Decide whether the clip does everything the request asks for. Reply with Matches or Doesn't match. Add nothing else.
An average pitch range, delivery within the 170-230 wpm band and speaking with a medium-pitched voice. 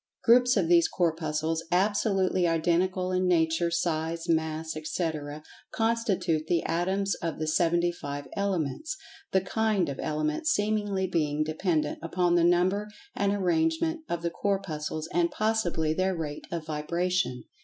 Doesn't match